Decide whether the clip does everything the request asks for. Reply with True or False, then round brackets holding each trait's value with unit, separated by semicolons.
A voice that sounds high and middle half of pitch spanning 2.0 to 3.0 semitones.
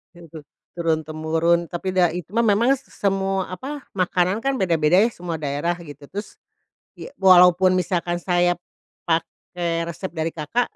False (175 Hz; 2.6 semitones)